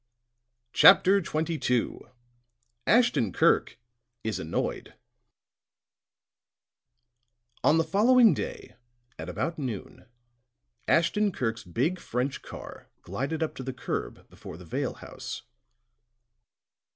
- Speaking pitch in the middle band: Yes, medium, 155 Hz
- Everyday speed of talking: No, slow, 95 wpm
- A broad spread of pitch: Yes, wide, 8.5 semitones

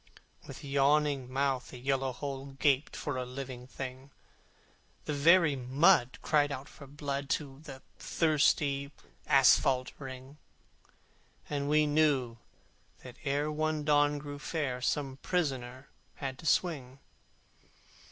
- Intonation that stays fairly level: Yes, narrow, 2.1 semitones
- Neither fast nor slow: No, slow, 125 wpm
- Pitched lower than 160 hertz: Yes, medium, 140 Hz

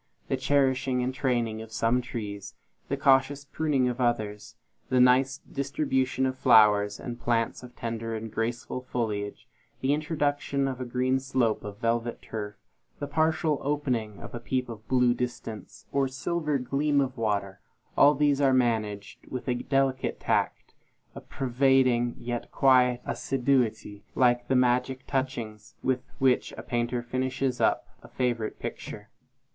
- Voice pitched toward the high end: No, low, 125 Hz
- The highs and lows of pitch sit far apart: No, narrow, 2.5 semitones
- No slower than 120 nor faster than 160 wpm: Yes, average, 150 wpm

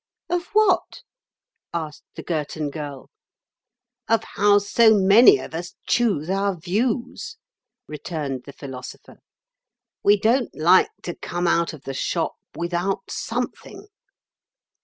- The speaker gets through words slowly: Yes, slow, 115 wpm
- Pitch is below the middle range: No, medium, 180 Hz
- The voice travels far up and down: Yes, wide, 6.0 semitones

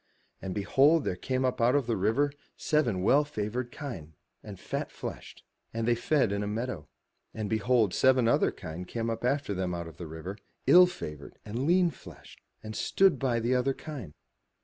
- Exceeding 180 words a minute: Yes, average, 190 wpm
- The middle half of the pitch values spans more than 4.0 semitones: Yes, average, 5.2 semitones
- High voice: No, low, 115 Hz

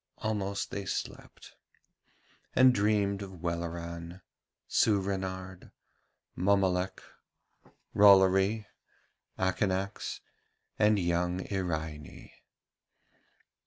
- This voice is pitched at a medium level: No, very low, 95 Hz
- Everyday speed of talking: No, slow, 60 wpm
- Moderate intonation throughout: No, narrow, 2.2 semitones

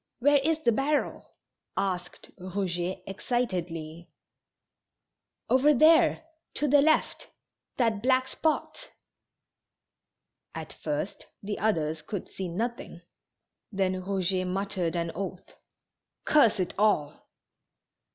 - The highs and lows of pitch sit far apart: Yes, wide, 6.2 semitones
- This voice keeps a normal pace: No, slow, 100 wpm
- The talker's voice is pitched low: No, high, 200 Hz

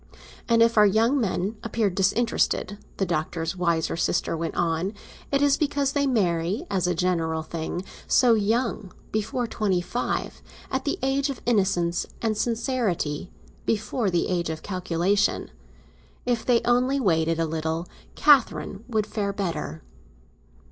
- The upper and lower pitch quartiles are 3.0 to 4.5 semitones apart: No, wide, 5.6 semitones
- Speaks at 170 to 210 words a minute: No, average, 140 wpm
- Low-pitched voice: No, high, 200 Hz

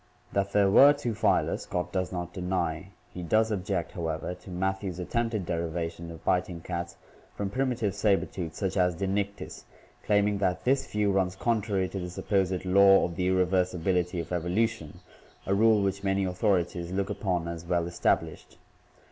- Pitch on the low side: Yes, very low, 95 Hz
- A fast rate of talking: No, average, 165 wpm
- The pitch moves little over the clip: Yes, narrow, 2.2 semitones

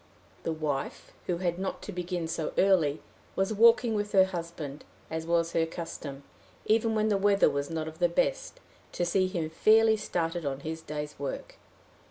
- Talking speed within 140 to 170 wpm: No, average, 180 wpm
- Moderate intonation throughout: Yes, average, 3.7 semitones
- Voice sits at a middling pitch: Yes, medium, 170 Hz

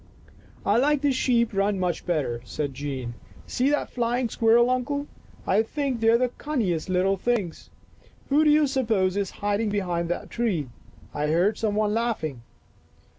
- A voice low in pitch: No, high, 215 Hz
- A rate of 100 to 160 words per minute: No, average, 175 wpm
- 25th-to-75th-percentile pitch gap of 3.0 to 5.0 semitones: No, wide, 5.5 semitones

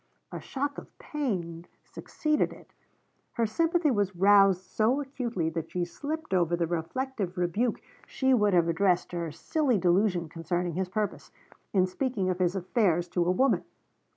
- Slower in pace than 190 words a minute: Yes, average, 160 wpm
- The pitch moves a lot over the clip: Yes, wide, 6.3 semitones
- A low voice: No, high, 190 Hz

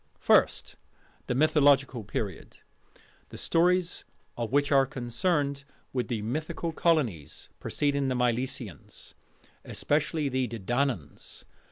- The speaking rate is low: Yes, slow, 100 wpm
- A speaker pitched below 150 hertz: Yes, low, 135 Hz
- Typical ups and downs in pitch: Yes, average, 3.7 semitones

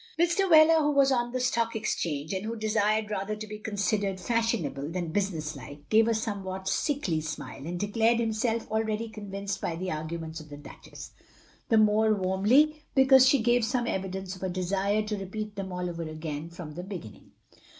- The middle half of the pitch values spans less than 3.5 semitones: No, average, 4.3 semitones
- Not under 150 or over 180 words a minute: No, average, 195 wpm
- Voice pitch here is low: No, high, 205 Hz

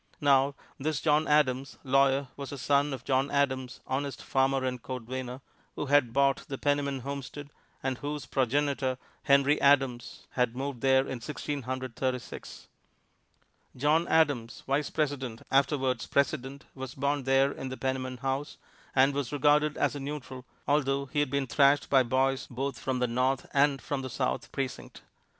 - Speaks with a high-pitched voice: No, low, 135 Hz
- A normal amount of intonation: No, narrow, 1.6 semitones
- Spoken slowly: No, average, 165 wpm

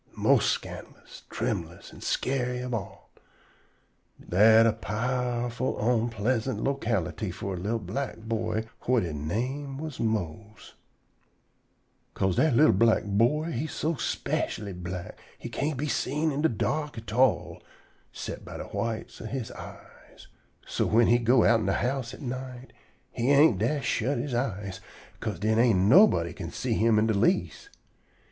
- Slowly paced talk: No, average, 155 wpm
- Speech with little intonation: No, average, 3.7 semitones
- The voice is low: Yes, low, 115 Hz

